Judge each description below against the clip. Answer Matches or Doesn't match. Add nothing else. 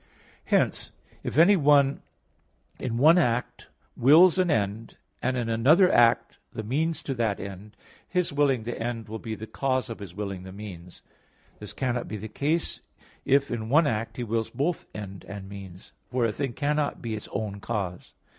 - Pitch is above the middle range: Doesn't match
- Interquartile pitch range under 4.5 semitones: Doesn't match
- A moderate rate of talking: Matches